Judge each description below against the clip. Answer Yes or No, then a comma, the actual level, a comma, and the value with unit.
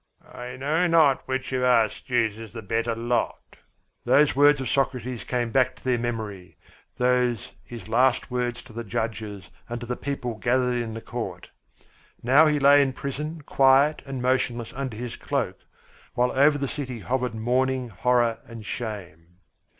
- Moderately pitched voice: No, low, 125 Hz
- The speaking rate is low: No, average, 165 wpm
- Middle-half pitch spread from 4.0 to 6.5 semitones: No, narrow, 2.6 semitones